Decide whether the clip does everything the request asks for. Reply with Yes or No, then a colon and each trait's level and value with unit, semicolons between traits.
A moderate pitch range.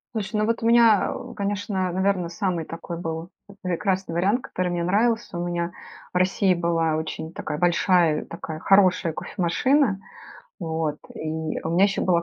Yes: average, 3.0 semitones